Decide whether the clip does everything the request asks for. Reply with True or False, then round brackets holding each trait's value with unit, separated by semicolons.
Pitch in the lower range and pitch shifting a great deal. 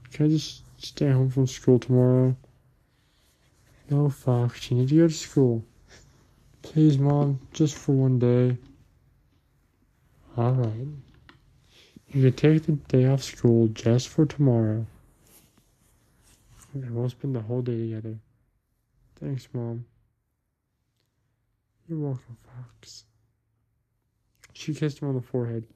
False (125 Hz; 2.7 semitones)